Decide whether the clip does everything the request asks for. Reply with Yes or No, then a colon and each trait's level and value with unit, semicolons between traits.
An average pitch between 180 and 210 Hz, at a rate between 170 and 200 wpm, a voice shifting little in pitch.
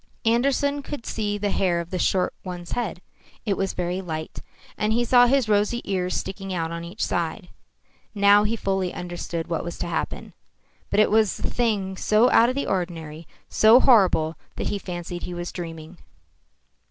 No: high, 190 Hz; average, 180 wpm; average, 4.0 semitones